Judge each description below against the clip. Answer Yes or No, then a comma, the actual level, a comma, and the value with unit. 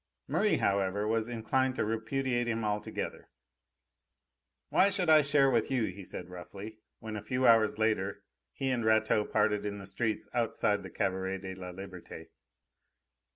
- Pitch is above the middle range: No, low, 110 Hz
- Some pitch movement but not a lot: Yes, average, 3.5 semitones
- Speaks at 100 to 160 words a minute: Yes, average, 155 wpm